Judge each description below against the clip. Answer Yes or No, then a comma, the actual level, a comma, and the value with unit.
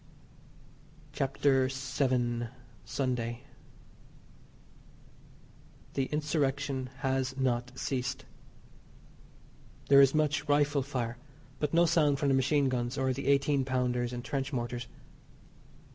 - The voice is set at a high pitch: No, low, 135 Hz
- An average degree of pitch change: No, narrow, 2.2 semitones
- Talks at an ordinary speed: No, slow, 100 wpm